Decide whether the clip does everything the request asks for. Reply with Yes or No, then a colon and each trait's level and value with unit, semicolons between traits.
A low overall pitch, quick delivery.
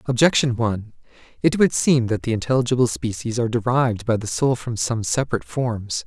No: low, 120 Hz; average, 180 wpm